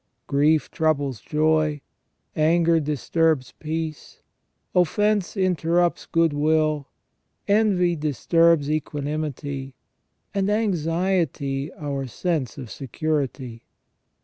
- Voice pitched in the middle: Yes, medium, 155 Hz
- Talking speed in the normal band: No, slow, 80 wpm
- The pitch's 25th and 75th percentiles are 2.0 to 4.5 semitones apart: Yes, average, 2.9 semitones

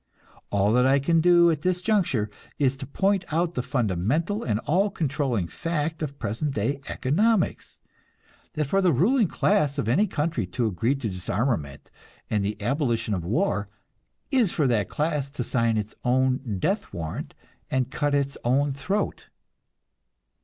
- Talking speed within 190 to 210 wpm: No, average, 160 wpm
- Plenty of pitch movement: Yes, wide, 6.5 semitones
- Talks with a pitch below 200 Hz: Yes, medium, 140 Hz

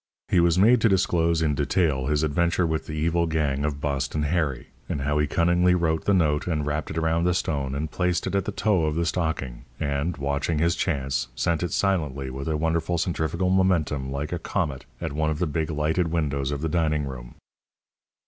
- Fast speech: Yes, fast, 210 wpm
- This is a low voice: Yes, very low, 80 Hz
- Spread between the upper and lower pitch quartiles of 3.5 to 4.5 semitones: No, average, 3.0 semitones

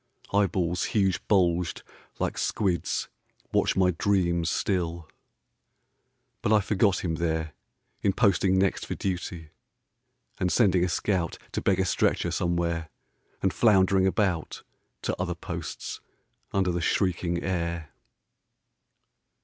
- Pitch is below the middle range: Yes, very low, 90 Hz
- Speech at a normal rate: No, slow, 115 wpm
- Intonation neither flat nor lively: No, narrow, 2.2 semitones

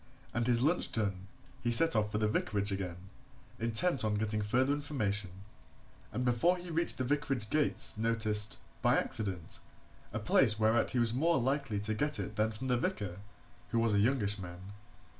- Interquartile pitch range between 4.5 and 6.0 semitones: No, average, 4.0 semitones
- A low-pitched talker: Yes, low, 110 Hz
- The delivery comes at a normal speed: Yes, average, 180 wpm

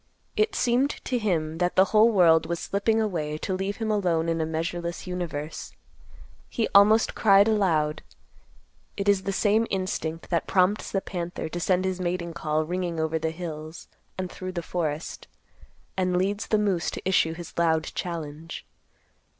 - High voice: No, medium, 180 Hz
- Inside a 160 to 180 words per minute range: Yes, average, 165 wpm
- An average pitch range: Yes, average, 3.5 semitones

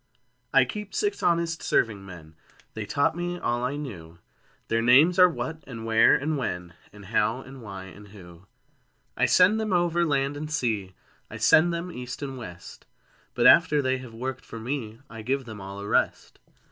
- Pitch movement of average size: No, wide, 7.0 semitones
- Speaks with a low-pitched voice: Yes, low, 125 Hz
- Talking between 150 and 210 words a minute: Yes, average, 185 wpm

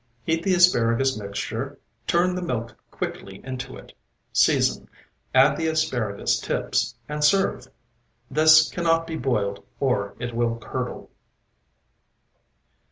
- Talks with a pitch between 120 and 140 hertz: Yes, low, 135 Hz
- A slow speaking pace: Yes, slow, 115 wpm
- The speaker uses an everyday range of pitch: No, wide, 6.0 semitones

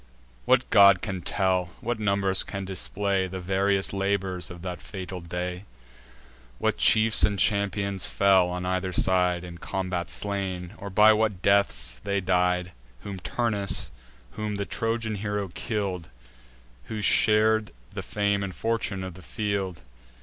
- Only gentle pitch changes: Yes, narrow, 2.1 semitones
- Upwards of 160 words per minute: No, average, 140 wpm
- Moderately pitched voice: No, very low, 95 Hz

